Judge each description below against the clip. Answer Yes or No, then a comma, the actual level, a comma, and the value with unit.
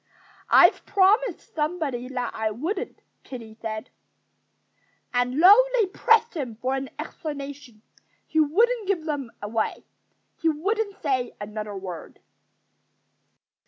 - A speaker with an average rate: No, slow, 115 wpm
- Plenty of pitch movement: Yes, wide, 8.0 semitones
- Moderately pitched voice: No, very high, 285 Hz